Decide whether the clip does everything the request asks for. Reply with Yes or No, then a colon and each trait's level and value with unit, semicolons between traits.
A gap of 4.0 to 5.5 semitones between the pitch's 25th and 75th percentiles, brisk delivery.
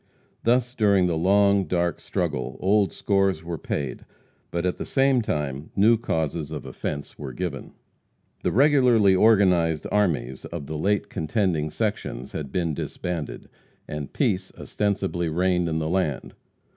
No: average, 4.6 semitones; average, 145 wpm